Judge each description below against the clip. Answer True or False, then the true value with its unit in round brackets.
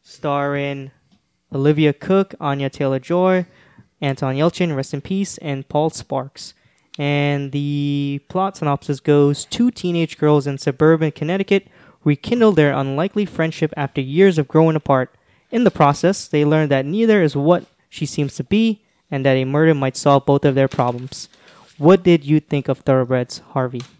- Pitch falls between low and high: True (150 Hz)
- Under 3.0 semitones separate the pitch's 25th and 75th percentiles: False (3.7 semitones)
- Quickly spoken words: False (160 wpm)